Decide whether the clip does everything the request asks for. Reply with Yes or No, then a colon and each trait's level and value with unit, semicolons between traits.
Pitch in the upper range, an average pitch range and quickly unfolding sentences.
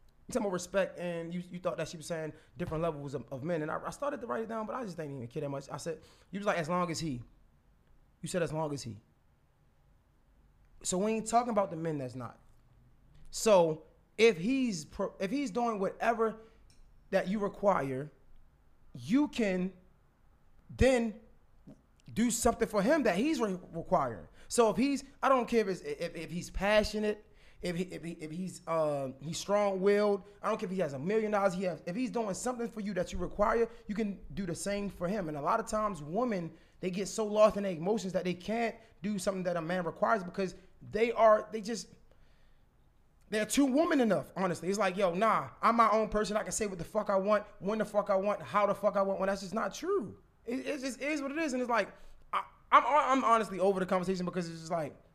Yes: high, 195 Hz; average, 4.6 semitones; fast, 225 wpm